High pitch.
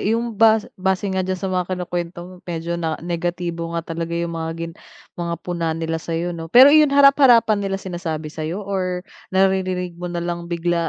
No: medium, 175 Hz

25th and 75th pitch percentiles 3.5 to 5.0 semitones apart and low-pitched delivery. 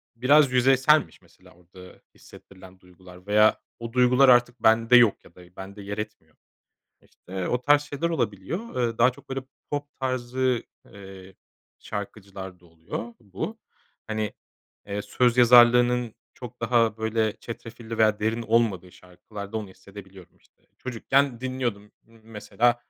Yes: average, 4.1 semitones; low, 115 Hz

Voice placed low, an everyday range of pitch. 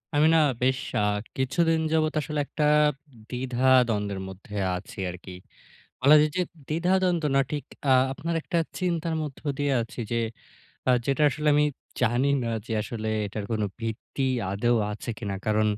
No: low, 130 Hz; wide, 5.7 semitones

